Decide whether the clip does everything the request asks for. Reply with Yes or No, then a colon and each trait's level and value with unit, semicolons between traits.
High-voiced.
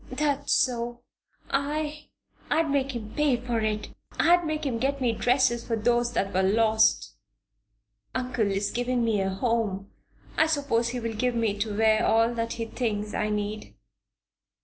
Yes: high, 235 Hz